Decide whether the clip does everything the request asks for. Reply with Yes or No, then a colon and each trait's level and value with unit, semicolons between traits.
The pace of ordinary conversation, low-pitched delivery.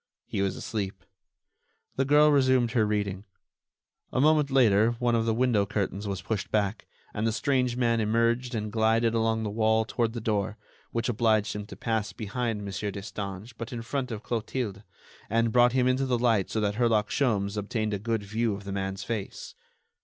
Yes: average, 190 wpm; low, 110 Hz